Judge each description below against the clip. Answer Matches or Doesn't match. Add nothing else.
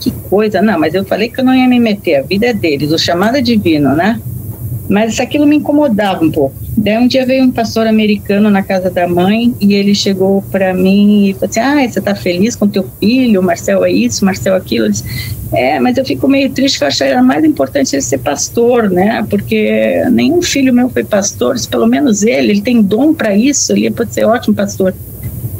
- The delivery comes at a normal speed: Doesn't match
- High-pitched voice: Matches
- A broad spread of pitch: Matches